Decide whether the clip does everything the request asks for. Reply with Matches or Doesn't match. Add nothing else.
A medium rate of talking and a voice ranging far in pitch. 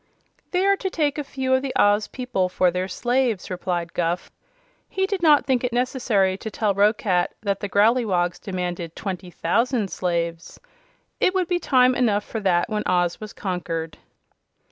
Matches